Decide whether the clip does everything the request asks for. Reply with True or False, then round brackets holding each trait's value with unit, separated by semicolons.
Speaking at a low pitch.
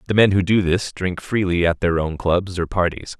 True (90 Hz)